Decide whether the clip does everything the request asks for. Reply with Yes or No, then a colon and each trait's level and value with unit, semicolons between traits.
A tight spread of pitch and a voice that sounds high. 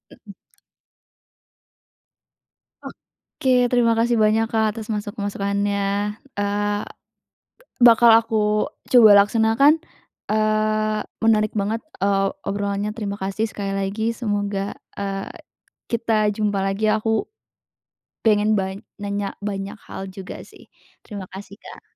Yes: narrow, 1.7 semitones; high, 210 Hz